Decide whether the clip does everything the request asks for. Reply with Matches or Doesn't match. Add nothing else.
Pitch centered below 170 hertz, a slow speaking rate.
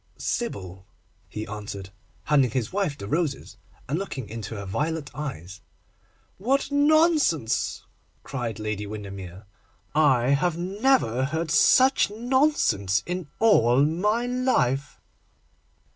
Matches